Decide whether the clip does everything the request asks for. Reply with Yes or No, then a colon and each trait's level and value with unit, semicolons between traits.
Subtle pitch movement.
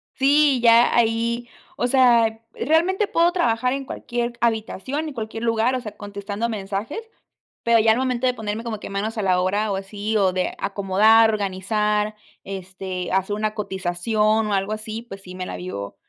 No: average, 3.2 semitones